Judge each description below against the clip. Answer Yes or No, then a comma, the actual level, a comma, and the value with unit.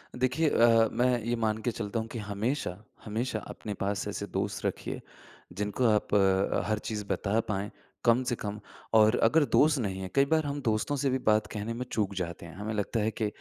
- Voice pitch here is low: Yes, low, 110 Hz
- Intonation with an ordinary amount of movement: Yes, average, 3.1 semitones